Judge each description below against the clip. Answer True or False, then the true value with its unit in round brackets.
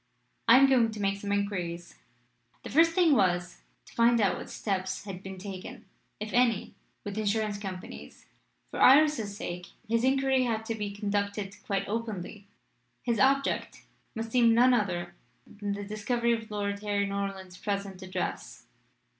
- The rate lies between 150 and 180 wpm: True (155 wpm)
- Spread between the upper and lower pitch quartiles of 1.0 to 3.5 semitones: True (2.8 semitones)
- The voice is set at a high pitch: True (205 Hz)